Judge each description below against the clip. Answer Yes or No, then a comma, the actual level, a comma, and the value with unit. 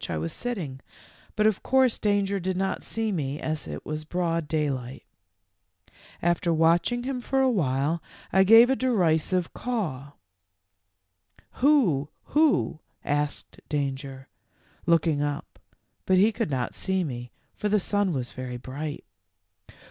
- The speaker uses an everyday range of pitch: No, wide, 6.6 semitones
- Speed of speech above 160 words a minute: No, average, 140 wpm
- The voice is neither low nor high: Yes, medium, 170 Hz